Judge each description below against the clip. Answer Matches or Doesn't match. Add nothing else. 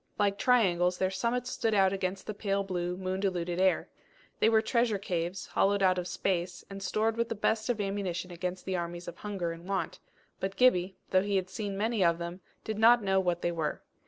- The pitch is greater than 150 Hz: Matches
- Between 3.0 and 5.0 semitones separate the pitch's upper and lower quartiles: Doesn't match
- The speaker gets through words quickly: Matches